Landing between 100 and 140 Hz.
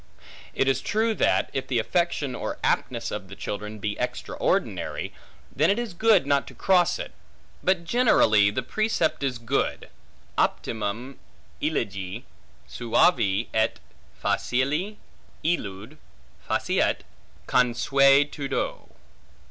Yes: low, 135 Hz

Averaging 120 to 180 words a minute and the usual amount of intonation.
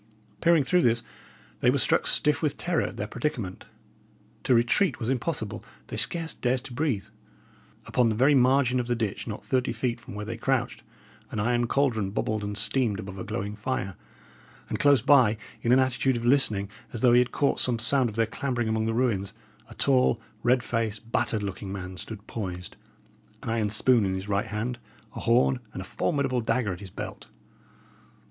No: average, 195 wpm; average, 3.5 semitones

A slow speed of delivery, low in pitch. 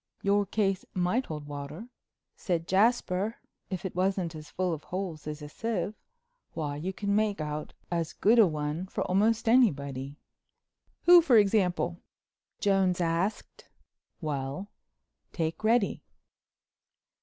No: slow, 125 wpm; medium, 185 Hz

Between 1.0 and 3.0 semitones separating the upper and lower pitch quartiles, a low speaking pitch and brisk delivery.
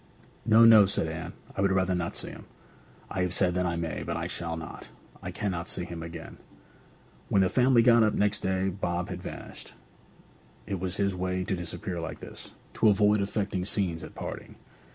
No: narrow, 2.6 semitones; very low, 95 Hz; average, 195 wpm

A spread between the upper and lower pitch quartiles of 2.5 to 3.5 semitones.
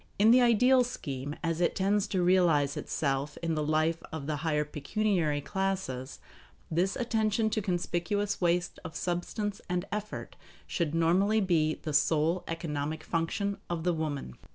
No: average, 4.6 semitones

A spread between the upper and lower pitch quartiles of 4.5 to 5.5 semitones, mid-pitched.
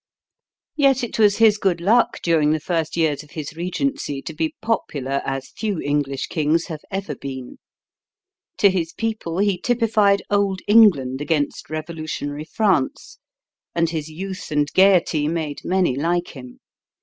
Yes: average, 5.2 semitones; medium, 165 Hz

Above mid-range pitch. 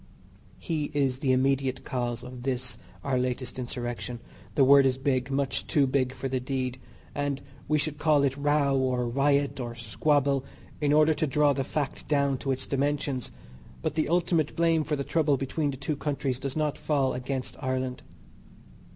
No: low, 135 Hz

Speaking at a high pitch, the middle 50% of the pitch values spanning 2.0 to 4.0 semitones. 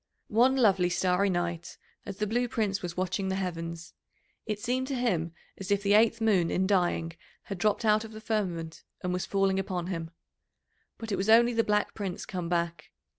Yes: high, 195 Hz; average, 3.6 semitones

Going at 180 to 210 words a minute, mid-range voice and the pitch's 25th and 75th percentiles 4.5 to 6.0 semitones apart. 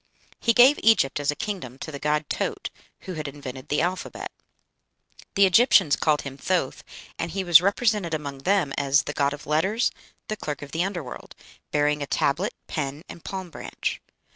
Yes: average, 185 wpm; medium, 155 Hz; average, 5.1 semitones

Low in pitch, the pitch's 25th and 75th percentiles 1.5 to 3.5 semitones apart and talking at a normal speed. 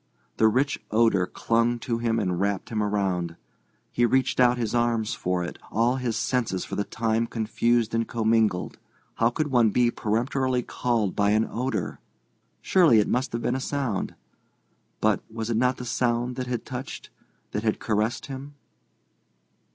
Yes: low, 115 Hz; narrow, 2.5 semitones; average, 165 wpm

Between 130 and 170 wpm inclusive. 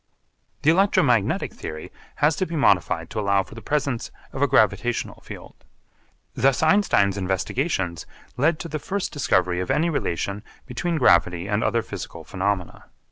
Yes: average, 150 wpm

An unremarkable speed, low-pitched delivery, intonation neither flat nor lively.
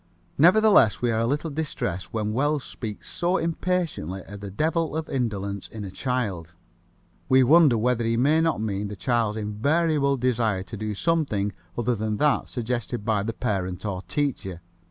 No: average, 165 wpm; low, 115 Hz; wide, 6.1 semitones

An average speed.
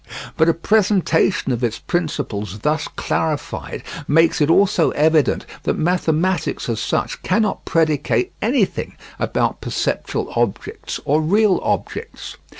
No: slow, 120 wpm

